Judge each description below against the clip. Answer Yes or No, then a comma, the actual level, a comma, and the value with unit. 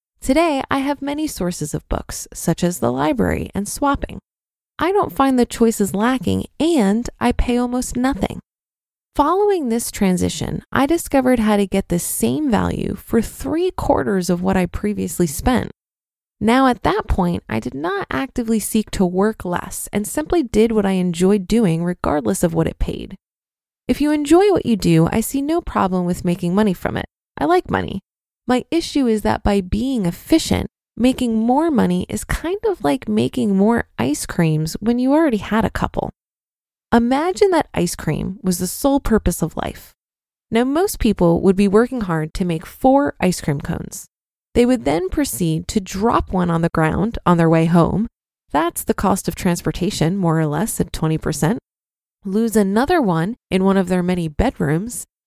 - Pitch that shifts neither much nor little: No, wide, 6.9 semitones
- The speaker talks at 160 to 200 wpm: Yes, average, 180 wpm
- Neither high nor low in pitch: No, high, 215 Hz